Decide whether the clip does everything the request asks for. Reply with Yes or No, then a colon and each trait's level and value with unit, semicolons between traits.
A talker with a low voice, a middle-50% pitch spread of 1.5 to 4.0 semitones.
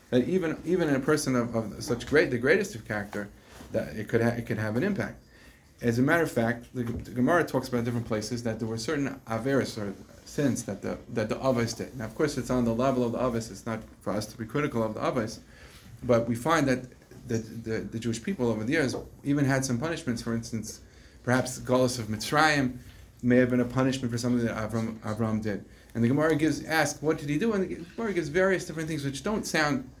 Yes: low, 120 Hz; average, 3.5 semitones